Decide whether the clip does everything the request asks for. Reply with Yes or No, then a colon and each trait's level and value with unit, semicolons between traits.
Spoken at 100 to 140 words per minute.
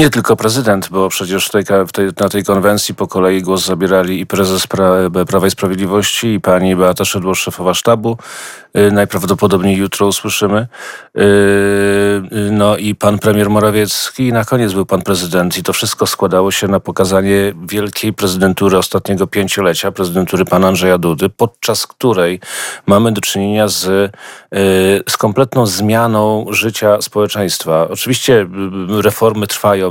Yes: average, 130 wpm